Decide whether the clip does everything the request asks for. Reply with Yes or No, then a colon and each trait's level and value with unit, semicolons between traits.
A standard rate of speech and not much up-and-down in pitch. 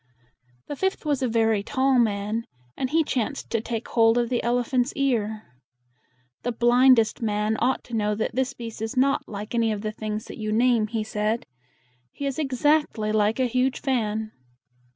No: average, 195 wpm; average, 3.1 semitones